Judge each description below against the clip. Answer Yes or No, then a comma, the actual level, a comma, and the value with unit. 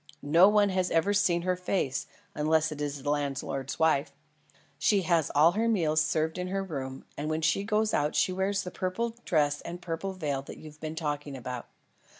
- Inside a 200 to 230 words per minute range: No, average, 190 wpm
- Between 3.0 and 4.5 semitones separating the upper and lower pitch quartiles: Yes, average, 4.1 semitones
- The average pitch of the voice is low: No, medium, 160 Hz